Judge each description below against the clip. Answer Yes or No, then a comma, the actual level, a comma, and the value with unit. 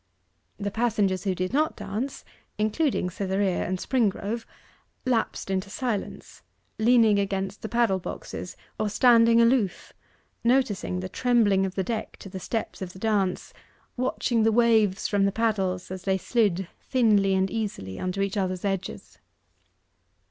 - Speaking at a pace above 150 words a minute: No, average, 145 wpm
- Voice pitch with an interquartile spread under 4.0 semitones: Yes, average, 3.3 semitones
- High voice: Yes, high, 205 Hz